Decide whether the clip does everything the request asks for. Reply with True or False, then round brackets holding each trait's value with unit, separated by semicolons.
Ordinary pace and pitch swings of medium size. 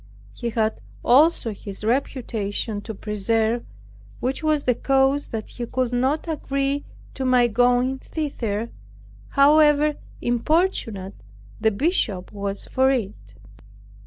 False (115 wpm; 4.2 semitones)